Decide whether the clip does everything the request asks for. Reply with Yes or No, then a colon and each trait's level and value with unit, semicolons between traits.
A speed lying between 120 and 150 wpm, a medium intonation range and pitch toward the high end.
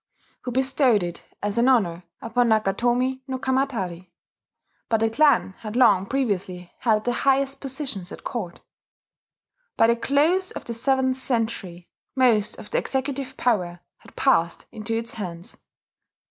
Yes: average, 145 wpm; average, 5.0 semitones; high, 235 Hz